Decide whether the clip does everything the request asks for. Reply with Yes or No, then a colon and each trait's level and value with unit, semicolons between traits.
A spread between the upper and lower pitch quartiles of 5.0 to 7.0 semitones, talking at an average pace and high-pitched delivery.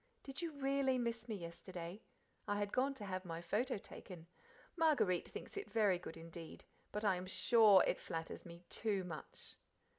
Yes: wide, 5.5 semitones; average, 175 wpm; high, 200 Hz